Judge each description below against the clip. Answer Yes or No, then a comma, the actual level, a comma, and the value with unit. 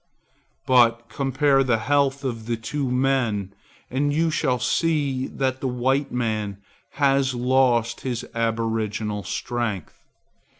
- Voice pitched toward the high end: No, low, 125 Hz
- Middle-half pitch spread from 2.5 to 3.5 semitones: Yes, average, 2.9 semitones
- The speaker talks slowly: Yes, slow, 120 wpm